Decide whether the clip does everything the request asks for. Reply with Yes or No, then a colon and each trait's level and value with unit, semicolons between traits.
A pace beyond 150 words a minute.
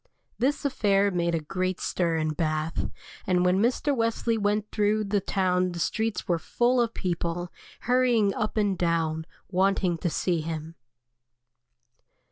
No: average, 145 wpm